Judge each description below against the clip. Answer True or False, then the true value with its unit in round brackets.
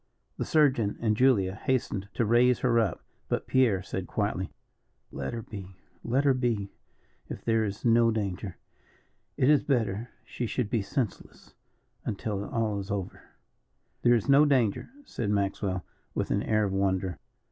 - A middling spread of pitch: True (3.6 semitones)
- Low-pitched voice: True (110 Hz)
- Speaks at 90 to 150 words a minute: False (160 wpm)